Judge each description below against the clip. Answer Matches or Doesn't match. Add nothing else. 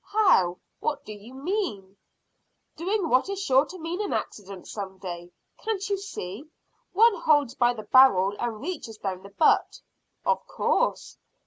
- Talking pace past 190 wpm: Doesn't match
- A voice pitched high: Matches